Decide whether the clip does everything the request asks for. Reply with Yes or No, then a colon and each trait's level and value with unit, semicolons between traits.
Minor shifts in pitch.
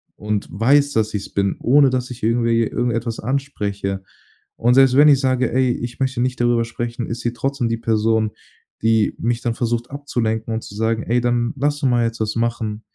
Yes: narrow, 2.2 semitones